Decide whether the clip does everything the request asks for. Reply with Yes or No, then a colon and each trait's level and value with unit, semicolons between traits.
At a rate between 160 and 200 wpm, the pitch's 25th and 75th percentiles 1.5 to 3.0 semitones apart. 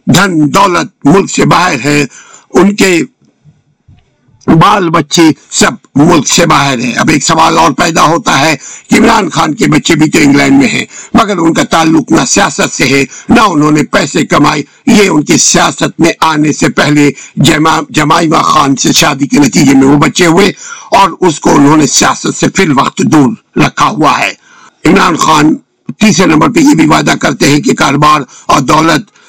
Yes: average, 170 wpm; average, 2.7 semitones